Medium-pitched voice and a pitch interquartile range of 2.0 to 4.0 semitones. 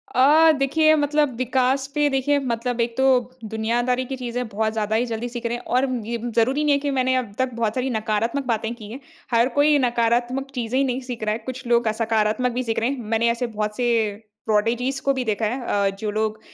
No: high, 240 Hz; average, 2.8 semitones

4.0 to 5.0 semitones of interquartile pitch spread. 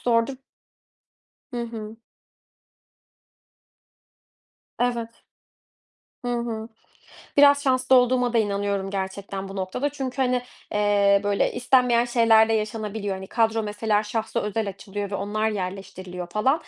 No: average, 3.2 semitones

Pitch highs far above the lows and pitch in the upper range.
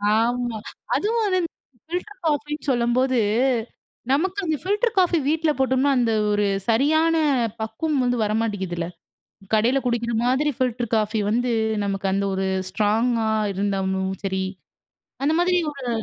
Yes: wide, 5.9 semitones; high, 245 Hz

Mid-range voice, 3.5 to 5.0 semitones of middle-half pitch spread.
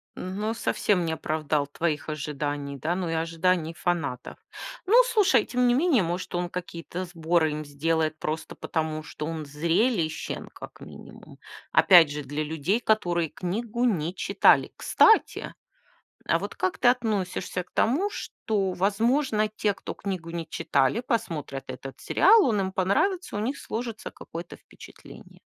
No: medium, 175 Hz; wide, 5.6 semitones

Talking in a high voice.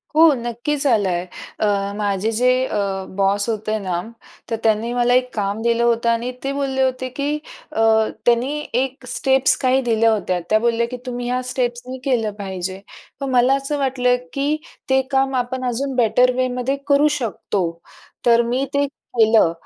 Yes: high, 245 Hz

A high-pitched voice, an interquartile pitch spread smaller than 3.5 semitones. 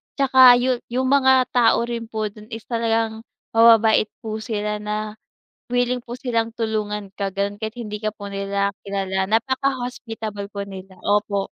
Yes: high, 220 Hz; average, 2.8 semitones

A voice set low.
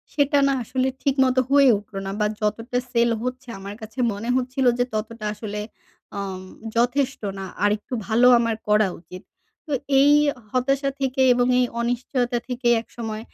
No: high, 240 Hz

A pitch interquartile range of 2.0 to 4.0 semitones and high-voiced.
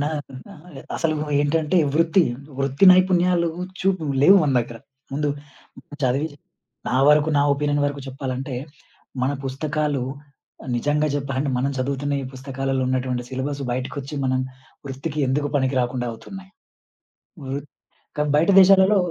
No: average, 2.9 semitones; medium, 140 Hz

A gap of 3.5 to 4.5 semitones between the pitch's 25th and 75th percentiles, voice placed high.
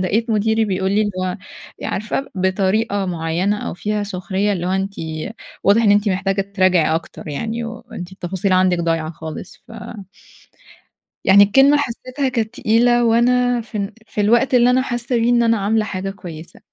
Yes: average, 3.8 semitones; high, 205 Hz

